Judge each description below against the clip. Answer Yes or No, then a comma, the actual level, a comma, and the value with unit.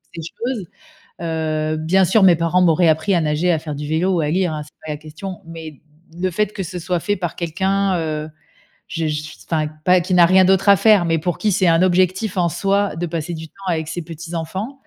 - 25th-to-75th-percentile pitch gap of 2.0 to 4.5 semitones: Yes, average, 2.8 semitones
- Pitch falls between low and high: Yes, medium, 170 Hz